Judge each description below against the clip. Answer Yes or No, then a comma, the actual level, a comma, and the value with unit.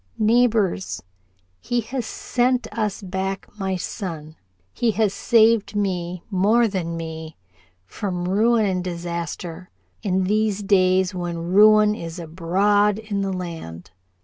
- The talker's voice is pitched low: No, high, 190 Hz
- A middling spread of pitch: Yes, average, 3.4 semitones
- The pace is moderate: No, slow, 120 wpm